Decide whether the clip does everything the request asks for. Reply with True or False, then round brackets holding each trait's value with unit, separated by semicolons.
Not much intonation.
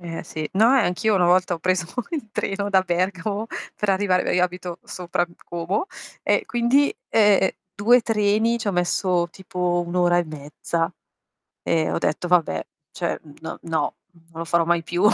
False (3.0 semitones)